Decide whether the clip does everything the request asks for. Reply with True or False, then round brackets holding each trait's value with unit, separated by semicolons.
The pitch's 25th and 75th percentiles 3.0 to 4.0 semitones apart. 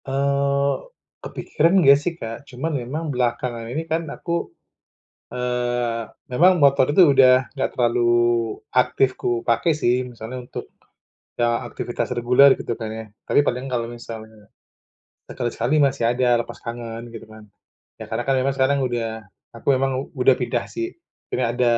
False (2.6 semitones)